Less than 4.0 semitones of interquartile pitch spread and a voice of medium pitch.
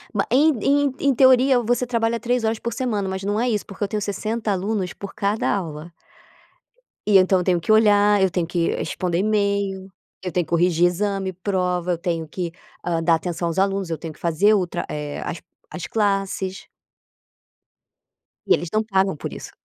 No: average, 3.5 semitones; high, 195 Hz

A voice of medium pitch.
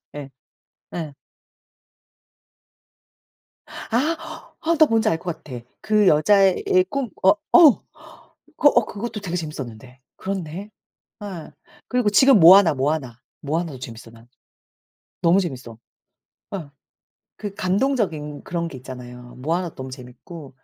Yes: medium, 170 Hz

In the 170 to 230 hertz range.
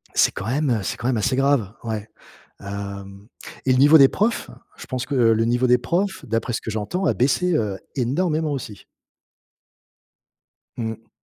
No: low, 125 Hz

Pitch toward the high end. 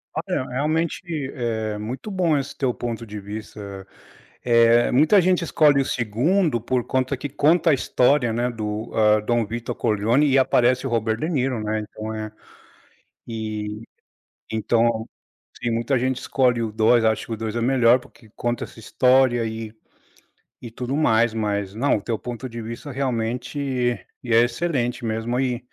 No: low, 120 Hz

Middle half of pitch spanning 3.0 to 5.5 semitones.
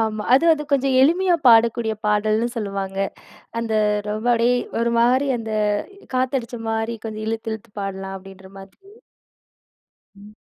No: narrow, 2.5 semitones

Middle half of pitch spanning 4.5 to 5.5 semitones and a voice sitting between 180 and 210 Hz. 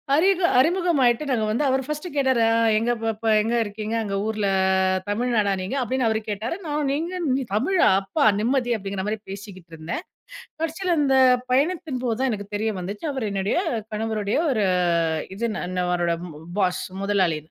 No: average, 5.1 semitones; high, 225 Hz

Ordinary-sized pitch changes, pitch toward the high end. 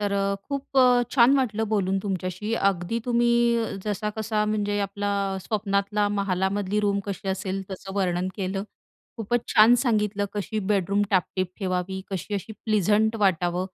No: narrow, 2.3 semitones; high, 205 Hz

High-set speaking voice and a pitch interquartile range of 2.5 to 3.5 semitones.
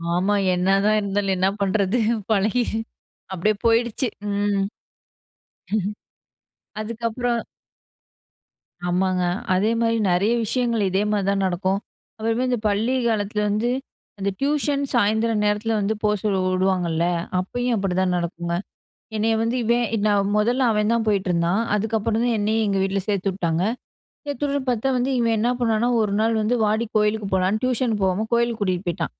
Yes: high, 210 Hz; average, 3.0 semitones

